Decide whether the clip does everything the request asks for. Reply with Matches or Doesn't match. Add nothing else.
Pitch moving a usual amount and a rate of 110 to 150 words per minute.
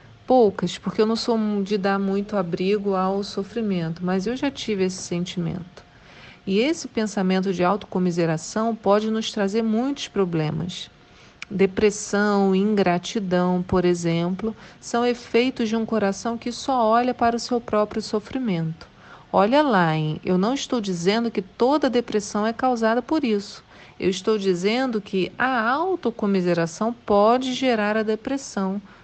Matches